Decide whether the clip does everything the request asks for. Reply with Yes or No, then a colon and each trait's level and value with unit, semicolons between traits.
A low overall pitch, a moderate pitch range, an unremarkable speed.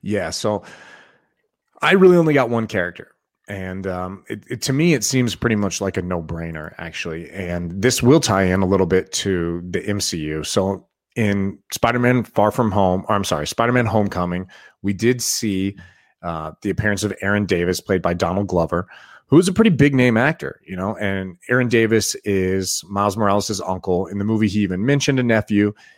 Yes: low, 100 Hz; average, 3.8 semitones; average, 195 wpm